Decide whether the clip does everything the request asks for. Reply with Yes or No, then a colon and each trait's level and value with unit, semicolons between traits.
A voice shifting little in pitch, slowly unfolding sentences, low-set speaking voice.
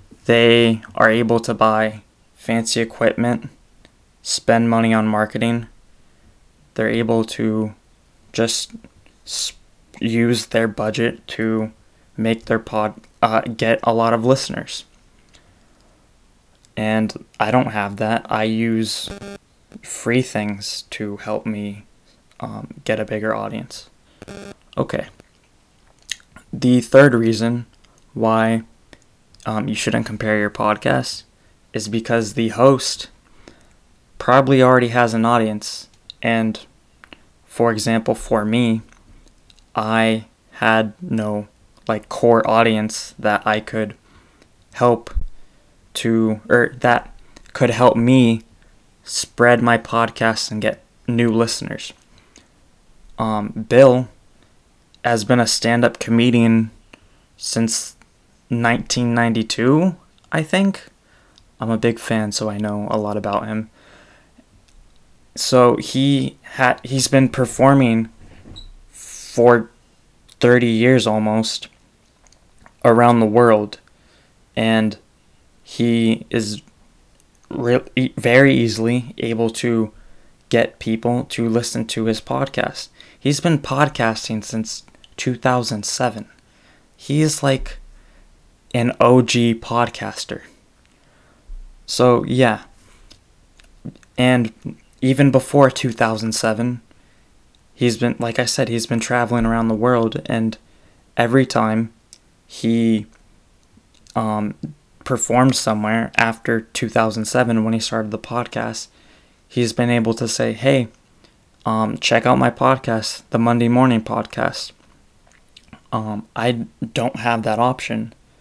Yes: narrow, 1.7 semitones; slow, 105 wpm; low, 115 Hz